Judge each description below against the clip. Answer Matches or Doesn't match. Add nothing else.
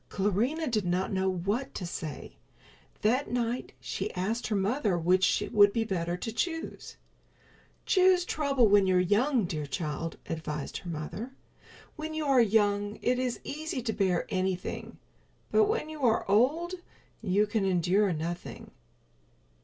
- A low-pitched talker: Doesn't match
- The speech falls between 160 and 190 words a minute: Doesn't match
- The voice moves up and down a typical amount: Doesn't match